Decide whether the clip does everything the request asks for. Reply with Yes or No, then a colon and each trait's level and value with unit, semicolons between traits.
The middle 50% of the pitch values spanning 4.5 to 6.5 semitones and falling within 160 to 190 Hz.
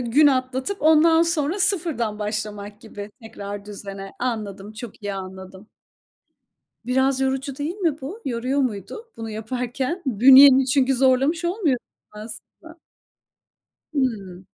No: wide, 5.4 semitones; very high, 255 Hz